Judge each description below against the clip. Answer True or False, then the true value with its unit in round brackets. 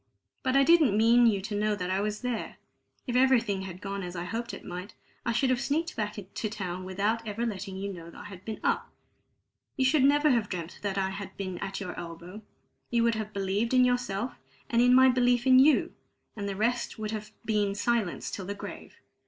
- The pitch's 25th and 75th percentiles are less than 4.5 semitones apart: True (3.9 semitones)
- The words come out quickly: True (220 wpm)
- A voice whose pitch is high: True (215 Hz)